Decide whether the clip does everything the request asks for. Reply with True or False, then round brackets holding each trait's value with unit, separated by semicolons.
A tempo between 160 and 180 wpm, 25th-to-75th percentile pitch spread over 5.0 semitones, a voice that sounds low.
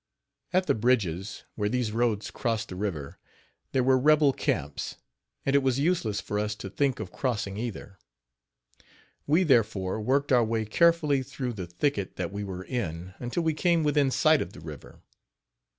True (170 wpm; 5.6 semitones; 120 Hz)